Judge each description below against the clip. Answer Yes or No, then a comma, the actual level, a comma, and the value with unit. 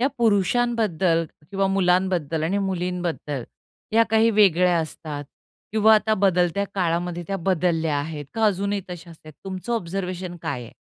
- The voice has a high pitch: No, medium, 180 Hz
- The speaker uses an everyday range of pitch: Yes, average, 3.2 semitones